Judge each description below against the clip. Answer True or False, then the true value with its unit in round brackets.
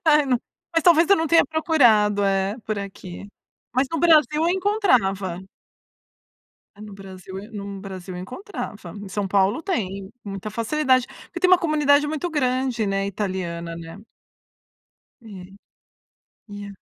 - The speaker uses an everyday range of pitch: False (7.8 semitones)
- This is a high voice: True (215 Hz)